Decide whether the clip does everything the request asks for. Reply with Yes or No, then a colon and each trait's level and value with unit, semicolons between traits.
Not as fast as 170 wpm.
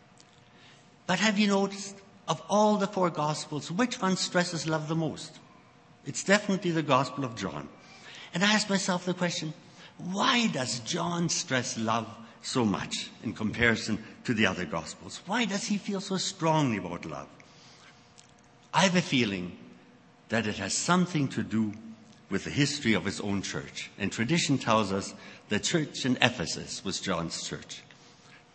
Yes: average, 160 wpm